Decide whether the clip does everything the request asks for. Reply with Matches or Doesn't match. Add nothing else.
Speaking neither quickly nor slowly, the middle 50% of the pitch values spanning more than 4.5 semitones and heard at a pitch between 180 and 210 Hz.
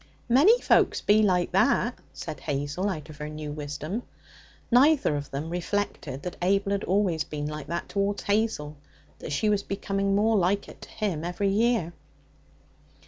Matches